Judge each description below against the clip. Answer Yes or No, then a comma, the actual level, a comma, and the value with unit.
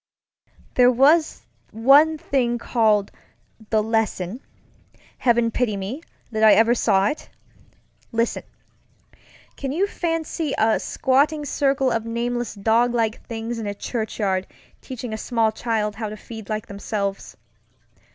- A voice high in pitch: Yes, high, 230 Hz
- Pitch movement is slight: No, average, 3.1 semitones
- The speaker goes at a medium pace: No, slow, 120 wpm